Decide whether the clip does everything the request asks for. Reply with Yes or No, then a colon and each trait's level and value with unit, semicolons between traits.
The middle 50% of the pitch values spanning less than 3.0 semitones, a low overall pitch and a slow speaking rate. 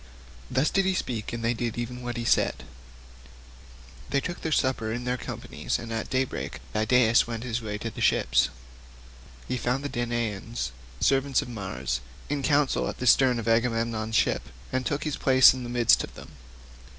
No: narrow, 2.5 semitones; low, 120 Hz; average, 185 wpm